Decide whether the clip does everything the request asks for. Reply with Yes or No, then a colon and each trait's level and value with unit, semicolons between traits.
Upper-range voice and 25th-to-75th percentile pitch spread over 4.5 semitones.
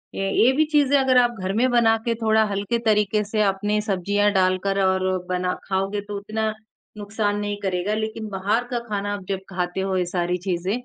No: high, 205 Hz; narrow, 2.5 semitones